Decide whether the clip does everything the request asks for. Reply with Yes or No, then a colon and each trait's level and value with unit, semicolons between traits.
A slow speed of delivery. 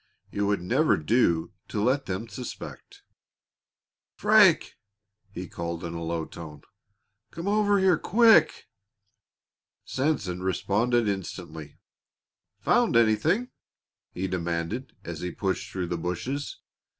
Yes: slow, 115 wpm